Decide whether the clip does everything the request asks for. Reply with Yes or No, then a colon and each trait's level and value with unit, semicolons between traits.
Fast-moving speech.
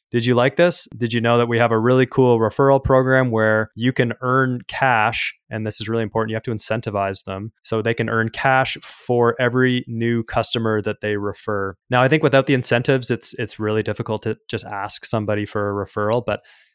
Yes: fast, 215 wpm